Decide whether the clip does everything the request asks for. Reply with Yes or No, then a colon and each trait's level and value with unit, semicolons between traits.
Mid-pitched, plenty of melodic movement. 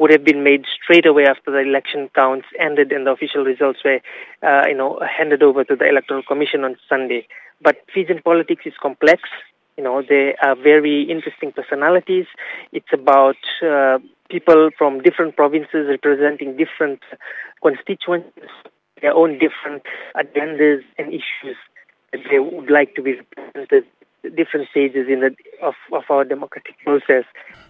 No: medium, 150 Hz; average, 3.6 semitones